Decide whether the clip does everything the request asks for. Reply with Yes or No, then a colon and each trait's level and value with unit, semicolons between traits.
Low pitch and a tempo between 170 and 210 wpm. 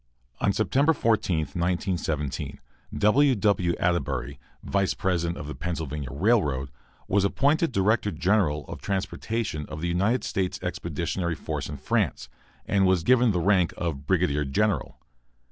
No: very low, 90 Hz; slow, 135 wpm